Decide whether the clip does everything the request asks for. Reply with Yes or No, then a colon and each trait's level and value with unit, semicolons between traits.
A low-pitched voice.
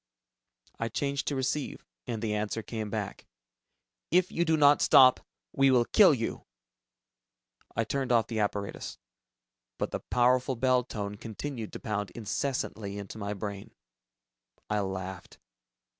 Yes: low, 115 Hz